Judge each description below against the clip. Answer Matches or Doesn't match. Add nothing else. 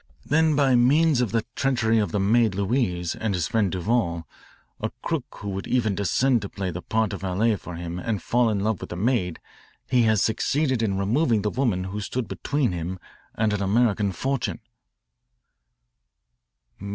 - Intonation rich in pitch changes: Doesn't match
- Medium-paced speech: Matches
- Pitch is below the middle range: Matches